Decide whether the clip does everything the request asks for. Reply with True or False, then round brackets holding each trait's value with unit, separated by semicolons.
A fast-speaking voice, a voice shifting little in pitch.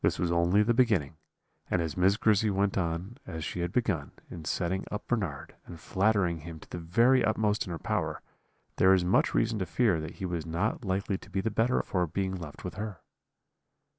False (210 wpm; 3.7 semitones)